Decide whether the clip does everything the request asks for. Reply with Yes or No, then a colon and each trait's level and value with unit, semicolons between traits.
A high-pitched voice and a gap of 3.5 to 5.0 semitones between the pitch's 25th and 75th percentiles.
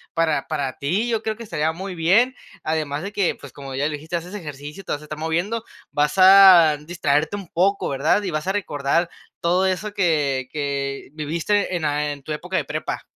No: medium, 160 Hz; average, 4.4 semitones